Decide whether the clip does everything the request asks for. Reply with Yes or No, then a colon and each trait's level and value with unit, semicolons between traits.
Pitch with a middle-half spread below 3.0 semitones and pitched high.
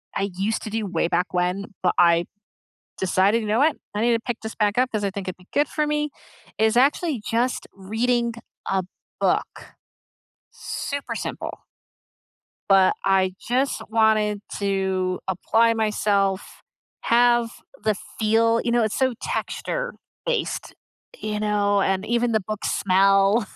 No: average, 3.4 semitones; high, 215 Hz